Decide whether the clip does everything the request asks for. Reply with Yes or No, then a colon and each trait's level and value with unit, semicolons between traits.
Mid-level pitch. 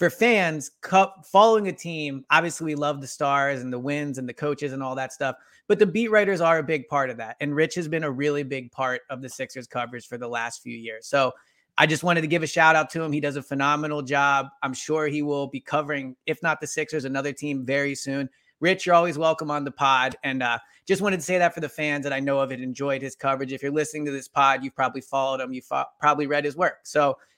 Yes: medium, 145 Hz